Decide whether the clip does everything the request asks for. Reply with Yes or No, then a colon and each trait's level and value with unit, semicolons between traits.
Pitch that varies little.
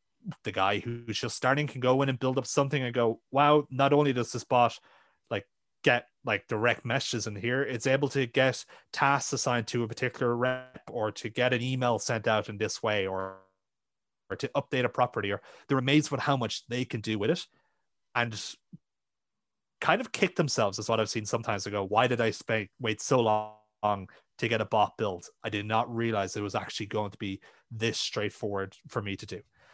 No: average, 3.3 semitones